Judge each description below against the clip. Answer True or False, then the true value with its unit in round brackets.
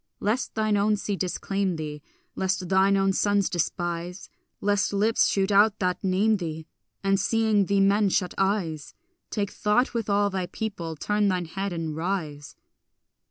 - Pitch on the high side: True (195 Hz)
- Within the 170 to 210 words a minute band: False (160 wpm)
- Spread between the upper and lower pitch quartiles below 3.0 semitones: True (2.5 semitones)